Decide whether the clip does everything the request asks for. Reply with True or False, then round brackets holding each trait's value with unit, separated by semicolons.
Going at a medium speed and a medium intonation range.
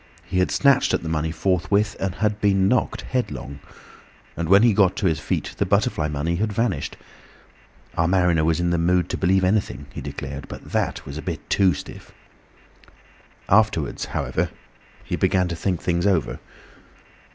True (175 wpm; 3.3 semitones)